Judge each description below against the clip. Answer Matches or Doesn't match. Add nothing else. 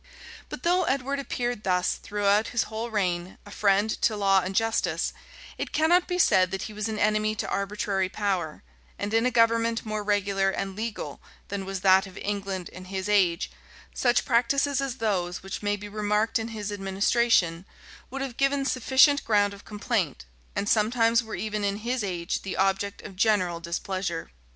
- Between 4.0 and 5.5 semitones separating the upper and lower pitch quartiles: Doesn't match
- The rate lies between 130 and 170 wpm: Doesn't match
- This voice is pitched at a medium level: Doesn't match